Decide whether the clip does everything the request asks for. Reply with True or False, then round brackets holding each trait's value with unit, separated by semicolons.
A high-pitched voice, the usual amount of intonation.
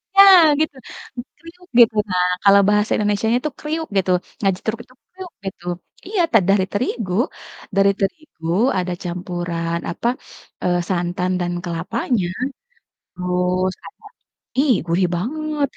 False (195 Hz; 6.1 semitones)